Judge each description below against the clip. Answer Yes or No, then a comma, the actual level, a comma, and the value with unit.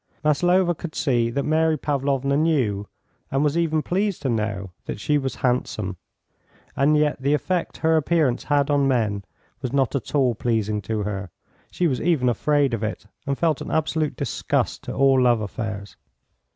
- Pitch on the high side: No, medium, 140 Hz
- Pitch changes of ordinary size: Yes, average, 4.9 semitones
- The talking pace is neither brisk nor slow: Yes, average, 175 wpm